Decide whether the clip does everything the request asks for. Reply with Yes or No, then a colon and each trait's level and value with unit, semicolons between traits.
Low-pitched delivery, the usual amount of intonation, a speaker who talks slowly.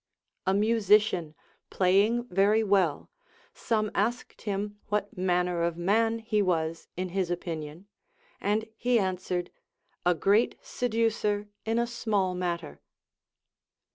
No: high, 200 Hz; average, 3.6 semitones; slow, 120 wpm